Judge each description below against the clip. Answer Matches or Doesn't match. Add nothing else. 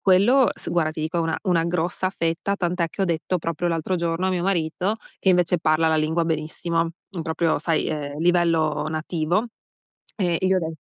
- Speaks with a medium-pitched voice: Matches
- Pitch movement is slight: Matches